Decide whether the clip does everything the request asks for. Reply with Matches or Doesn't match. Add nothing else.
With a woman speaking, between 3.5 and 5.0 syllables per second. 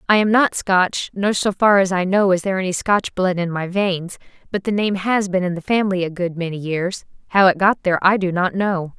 Doesn't match